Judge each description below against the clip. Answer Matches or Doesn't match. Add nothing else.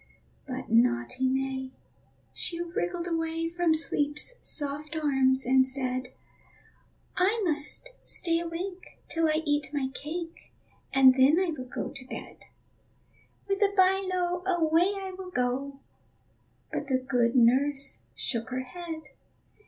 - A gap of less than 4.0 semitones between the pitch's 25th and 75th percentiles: Doesn't match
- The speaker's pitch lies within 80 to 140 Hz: Doesn't match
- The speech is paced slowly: Matches